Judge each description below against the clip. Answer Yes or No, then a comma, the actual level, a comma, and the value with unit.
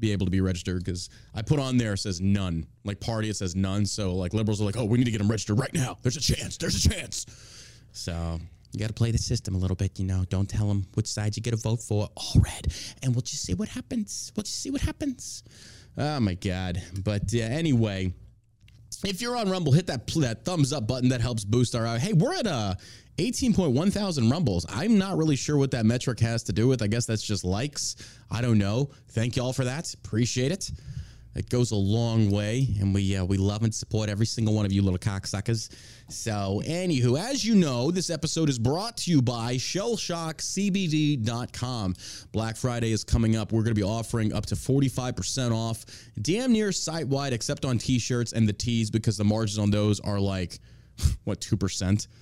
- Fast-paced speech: Yes, fast, 220 wpm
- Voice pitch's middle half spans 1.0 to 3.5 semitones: No, average, 4.0 semitones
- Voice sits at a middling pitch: No, low, 115 Hz